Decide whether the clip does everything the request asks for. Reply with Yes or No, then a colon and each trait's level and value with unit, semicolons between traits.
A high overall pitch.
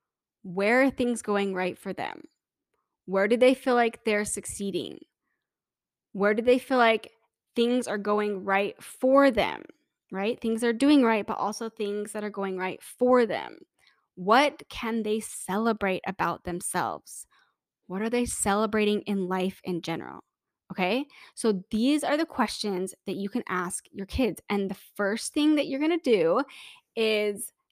Yes: high, 220 Hz